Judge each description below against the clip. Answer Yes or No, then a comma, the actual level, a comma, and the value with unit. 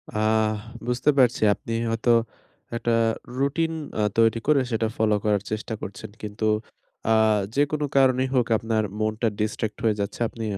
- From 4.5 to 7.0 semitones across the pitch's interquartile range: No, average, 2.9 semitones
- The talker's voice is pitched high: No, low, 115 Hz